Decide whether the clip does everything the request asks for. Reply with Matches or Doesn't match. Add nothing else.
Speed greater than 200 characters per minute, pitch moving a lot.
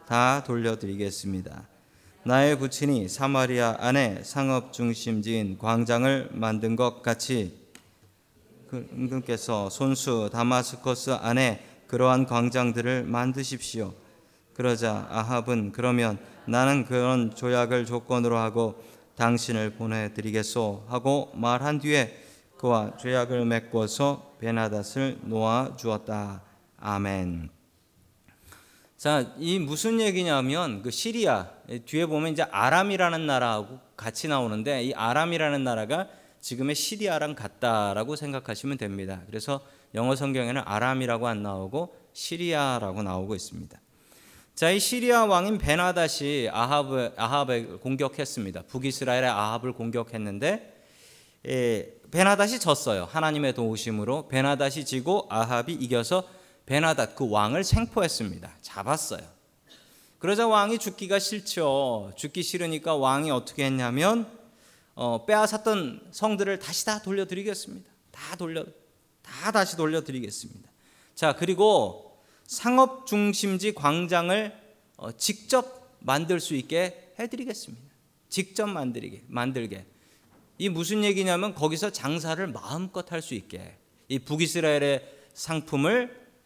Matches